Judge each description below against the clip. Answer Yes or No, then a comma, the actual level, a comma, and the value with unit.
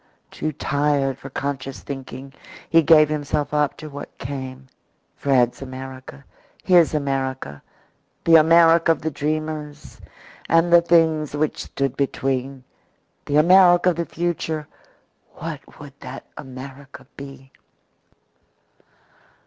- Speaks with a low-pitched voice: No, medium, 145 Hz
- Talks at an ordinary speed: No, slow, 115 wpm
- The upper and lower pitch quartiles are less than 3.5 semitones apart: Yes, average, 2.9 semitones